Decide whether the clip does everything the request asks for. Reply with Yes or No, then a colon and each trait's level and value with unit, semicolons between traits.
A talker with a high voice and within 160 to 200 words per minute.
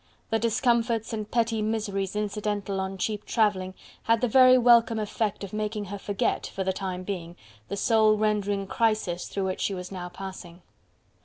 Yes: high, 210 Hz; average, 170 wpm